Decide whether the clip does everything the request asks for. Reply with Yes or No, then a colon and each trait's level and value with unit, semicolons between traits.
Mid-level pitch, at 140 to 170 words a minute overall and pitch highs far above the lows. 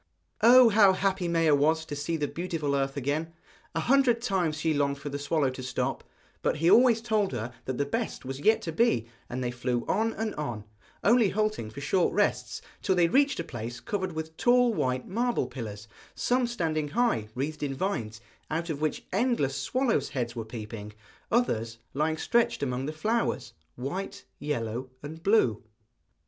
No: medium, 155 Hz; average, 180 wpm; wide, 8.3 semitones